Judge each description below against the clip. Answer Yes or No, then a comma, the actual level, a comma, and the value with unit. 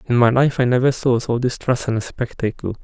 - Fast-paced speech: Yes, fast, 210 wpm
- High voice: No, low, 120 Hz